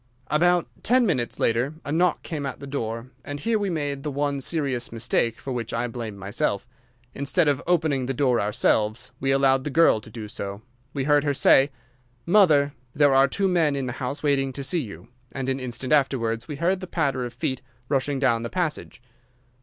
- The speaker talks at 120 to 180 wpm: No, average, 200 wpm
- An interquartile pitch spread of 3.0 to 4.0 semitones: Yes, average, 3.6 semitones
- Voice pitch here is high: No, low, 135 Hz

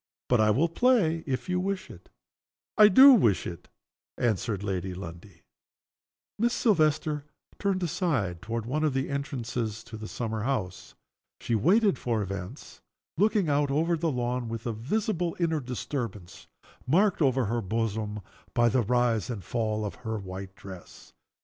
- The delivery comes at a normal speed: Yes, average, 155 wpm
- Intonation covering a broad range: Yes, wide, 7.0 semitones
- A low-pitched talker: Yes, low, 125 Hz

